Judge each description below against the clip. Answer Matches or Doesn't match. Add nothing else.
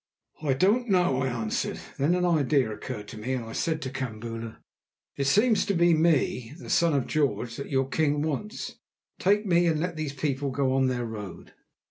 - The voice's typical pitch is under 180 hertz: Matches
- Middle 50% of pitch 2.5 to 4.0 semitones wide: Doesn't match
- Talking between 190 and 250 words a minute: Matches